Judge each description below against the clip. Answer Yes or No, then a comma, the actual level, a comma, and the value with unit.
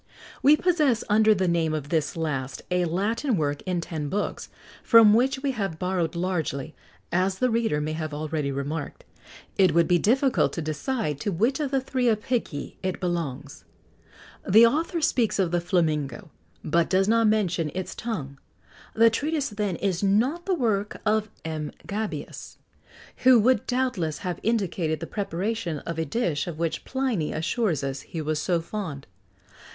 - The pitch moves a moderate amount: No, wide, 6.3 semitones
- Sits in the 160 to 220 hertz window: Yes, medium, 185 Hz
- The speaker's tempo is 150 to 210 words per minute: Yes, average, 165 wpm